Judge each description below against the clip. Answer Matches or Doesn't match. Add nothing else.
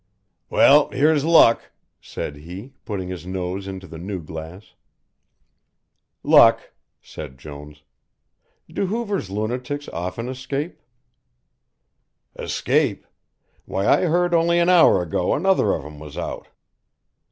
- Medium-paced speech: Doesn't match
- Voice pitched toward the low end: Matches